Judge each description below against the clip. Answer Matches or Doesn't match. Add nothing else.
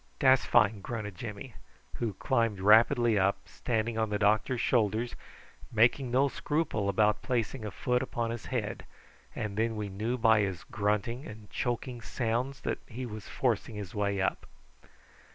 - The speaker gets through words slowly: Doesn't match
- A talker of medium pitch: Doesn't match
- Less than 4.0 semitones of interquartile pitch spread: Matches